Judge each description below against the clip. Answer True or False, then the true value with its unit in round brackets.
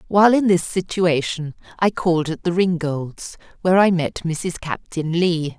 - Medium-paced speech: True (160 wpm)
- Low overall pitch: False (170 Hz)